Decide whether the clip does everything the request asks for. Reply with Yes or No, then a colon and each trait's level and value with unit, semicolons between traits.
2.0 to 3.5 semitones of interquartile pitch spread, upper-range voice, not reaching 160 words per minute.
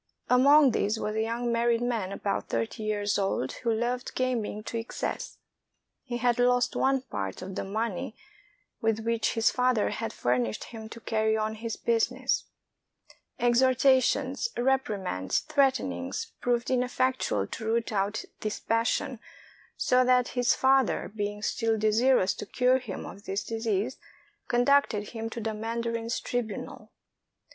Yes: average, 2.8 semitones; high, 230 Hz; average, 145 wpm